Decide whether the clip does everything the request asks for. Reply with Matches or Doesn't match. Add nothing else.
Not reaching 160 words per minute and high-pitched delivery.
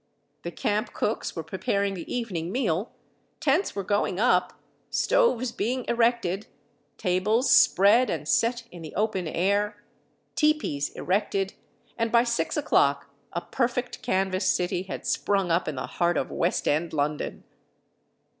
Matches